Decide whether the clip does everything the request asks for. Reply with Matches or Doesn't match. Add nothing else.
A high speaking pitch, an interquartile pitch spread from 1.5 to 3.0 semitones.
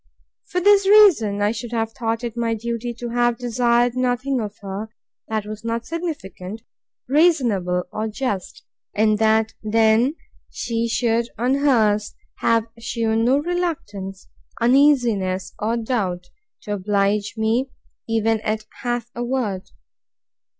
Matches